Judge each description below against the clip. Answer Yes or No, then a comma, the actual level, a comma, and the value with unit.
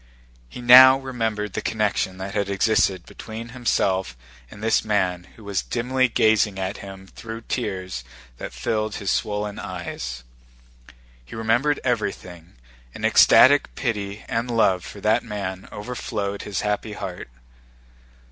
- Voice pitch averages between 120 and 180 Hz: No, low, 105 Hz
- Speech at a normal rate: No, slow, 130 wpm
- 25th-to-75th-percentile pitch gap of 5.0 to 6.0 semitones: No, average, 3.1 semitones